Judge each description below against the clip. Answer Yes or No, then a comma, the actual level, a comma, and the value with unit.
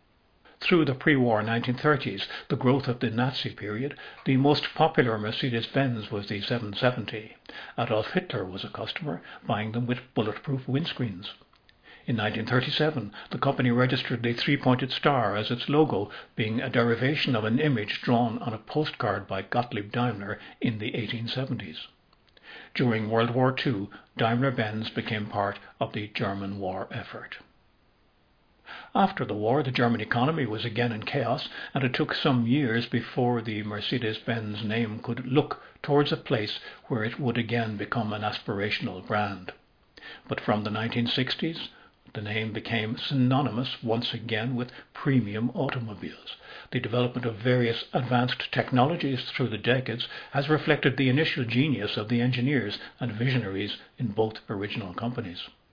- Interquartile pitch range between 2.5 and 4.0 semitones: Yes, average, 3.1 semitones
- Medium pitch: No, low, 120 Hz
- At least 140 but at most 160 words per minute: Yes, average, 150 wpm